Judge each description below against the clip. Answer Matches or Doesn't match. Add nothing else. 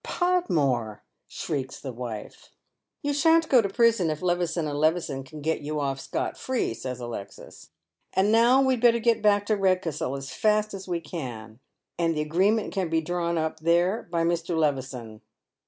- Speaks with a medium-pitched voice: Matches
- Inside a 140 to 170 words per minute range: Doesn't match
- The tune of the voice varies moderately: Doesn't match